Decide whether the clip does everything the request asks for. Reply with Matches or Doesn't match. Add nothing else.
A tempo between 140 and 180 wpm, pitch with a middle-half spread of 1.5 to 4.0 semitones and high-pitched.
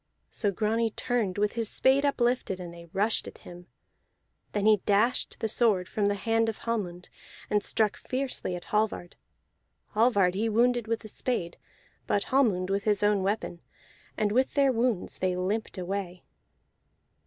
Matches